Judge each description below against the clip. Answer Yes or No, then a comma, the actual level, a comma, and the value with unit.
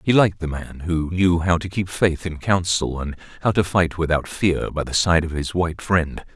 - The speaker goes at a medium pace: No, fast, 235 wpm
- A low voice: Yes, very low, 85 Hz